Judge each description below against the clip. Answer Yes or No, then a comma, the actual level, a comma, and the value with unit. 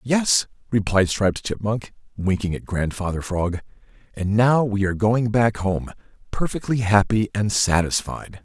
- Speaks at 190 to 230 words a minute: No, slow, 135 wpm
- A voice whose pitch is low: Yes, low, 105 Hz